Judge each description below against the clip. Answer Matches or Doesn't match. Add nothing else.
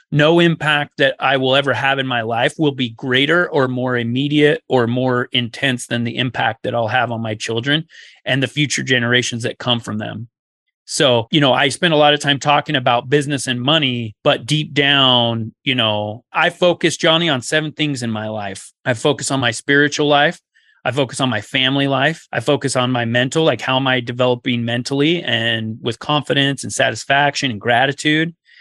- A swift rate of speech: Doesn't match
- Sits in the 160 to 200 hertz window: Doesn't match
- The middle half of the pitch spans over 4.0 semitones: Doesn't match